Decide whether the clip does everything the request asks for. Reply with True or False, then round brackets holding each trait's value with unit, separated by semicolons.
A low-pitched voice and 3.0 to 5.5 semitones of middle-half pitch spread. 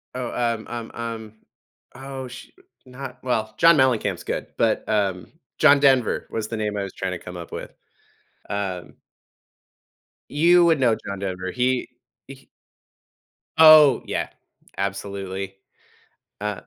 True (115 Hz; 4.9 semitones)